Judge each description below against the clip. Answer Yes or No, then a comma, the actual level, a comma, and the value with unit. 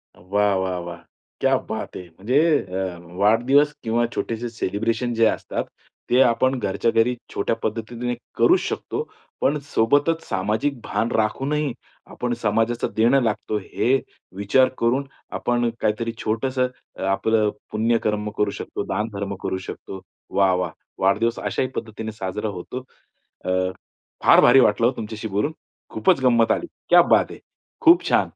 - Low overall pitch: Yes, low, 115 Hz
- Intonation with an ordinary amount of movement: Yes, average, 3.1 semitones